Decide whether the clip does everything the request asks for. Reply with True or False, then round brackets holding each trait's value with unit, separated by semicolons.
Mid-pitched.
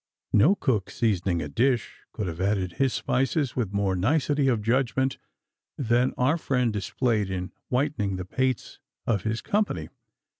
False (120 Hz)